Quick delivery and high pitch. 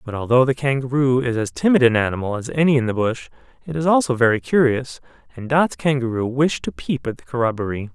No: fast, 210 wpm; low, 130 Hz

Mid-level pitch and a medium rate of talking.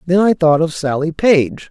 No: medium, 165 Hz; fast, 210 wpm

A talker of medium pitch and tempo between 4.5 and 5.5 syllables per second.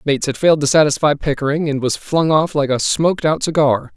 No: medium, 150 Hz; 6.0 syllables/s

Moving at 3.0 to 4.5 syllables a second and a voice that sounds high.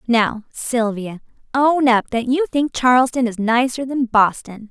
Yes: 4.1 syllables/s; high, 245 Hz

